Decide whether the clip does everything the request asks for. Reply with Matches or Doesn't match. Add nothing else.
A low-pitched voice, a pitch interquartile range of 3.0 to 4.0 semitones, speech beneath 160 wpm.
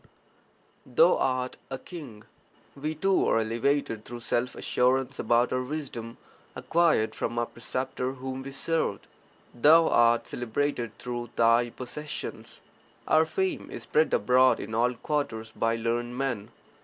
Matches